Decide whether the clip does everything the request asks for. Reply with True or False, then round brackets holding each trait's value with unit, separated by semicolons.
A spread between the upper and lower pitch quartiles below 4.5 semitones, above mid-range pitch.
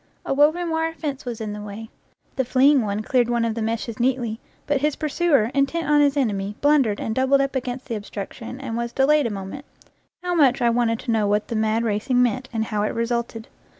True (3.8 semitones; 245 Hz)